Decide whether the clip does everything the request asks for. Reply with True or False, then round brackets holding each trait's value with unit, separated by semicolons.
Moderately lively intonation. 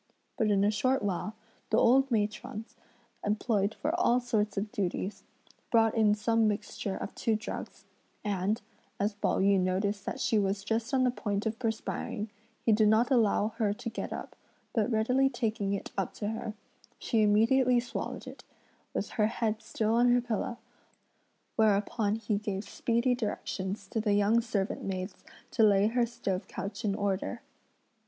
False (2.3 semitones)